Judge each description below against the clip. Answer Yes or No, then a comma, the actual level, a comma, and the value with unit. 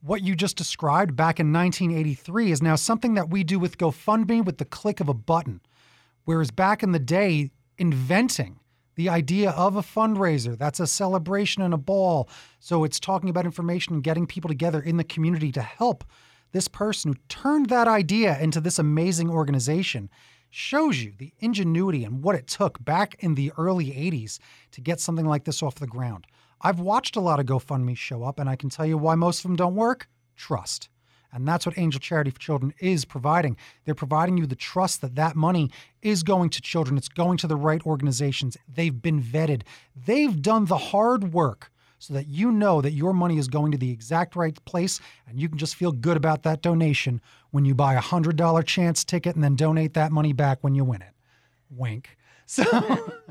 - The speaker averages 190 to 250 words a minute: Yes, fast, 205 wpm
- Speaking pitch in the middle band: Yes, medium, 160 Hz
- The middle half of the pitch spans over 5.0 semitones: No, average, 4.5 semitones